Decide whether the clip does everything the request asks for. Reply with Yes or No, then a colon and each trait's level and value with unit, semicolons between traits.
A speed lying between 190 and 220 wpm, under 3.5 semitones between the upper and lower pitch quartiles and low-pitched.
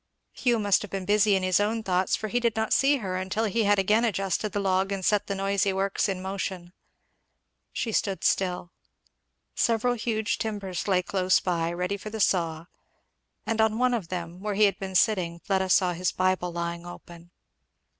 No: average, 195 wpm; narrow, 2.6 semitones; high, 195 Hz